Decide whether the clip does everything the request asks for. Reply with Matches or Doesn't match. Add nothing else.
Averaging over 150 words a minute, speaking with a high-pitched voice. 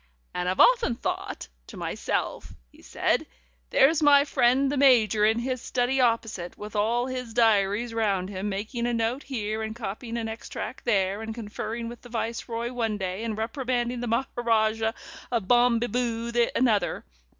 Matches